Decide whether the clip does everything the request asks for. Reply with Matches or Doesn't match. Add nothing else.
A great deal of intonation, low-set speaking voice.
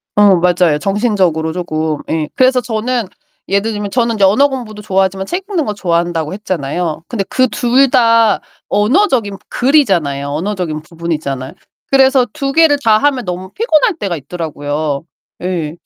Doesn't match